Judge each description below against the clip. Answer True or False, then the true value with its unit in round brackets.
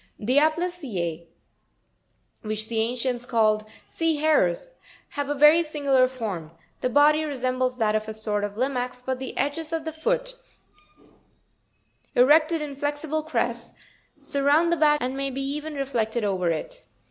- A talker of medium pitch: False (270 Hz)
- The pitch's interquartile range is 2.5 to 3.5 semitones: False (5.1 semitones)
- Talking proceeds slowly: False (150 wpm)